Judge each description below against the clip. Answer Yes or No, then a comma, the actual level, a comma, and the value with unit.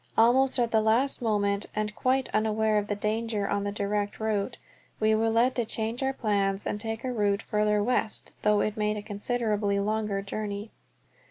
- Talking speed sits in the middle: Yes, average, 185 wpm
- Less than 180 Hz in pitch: No, high, 215 Hz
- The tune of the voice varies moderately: No, narrow, 1.6 semitones